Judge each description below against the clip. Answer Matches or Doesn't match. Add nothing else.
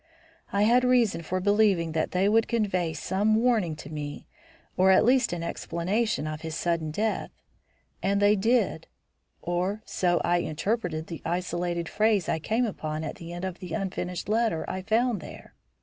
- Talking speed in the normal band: Matches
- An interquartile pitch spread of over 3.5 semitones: Matches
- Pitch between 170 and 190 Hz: Matches